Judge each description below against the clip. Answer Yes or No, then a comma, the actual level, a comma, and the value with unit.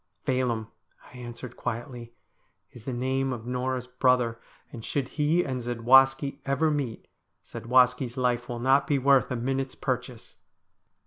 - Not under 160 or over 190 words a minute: No, average, 150 wpm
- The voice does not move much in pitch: Yes, narrow, 1.8 semitones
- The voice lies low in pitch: Yes, low, 125 Hz